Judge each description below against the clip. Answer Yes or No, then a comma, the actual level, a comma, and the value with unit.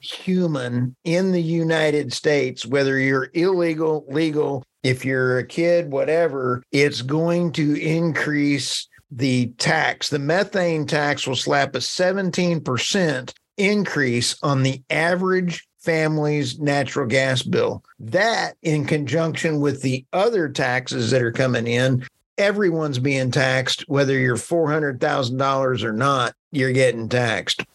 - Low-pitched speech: No, medium, 145 Hz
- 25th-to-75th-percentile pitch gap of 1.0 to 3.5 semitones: No, average, 3.9 semitones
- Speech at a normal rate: No, slow, 125 wpm